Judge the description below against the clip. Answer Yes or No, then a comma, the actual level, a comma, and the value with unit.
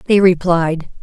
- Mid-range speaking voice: Yes, medium, 175 Hz